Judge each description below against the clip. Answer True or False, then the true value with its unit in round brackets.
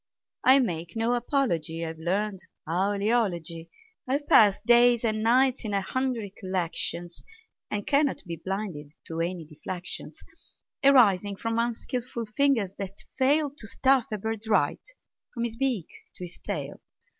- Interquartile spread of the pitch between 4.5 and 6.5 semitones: True (5.2 semitones)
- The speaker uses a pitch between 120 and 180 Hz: False (210 Hz)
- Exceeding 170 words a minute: False (145 wpm)